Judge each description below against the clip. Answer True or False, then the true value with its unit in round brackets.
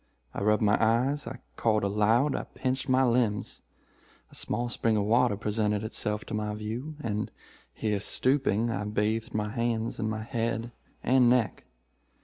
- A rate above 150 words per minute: True (160 wpm)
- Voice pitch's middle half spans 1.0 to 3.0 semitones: True (2.4 semitones)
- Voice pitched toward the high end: False (110 Hz)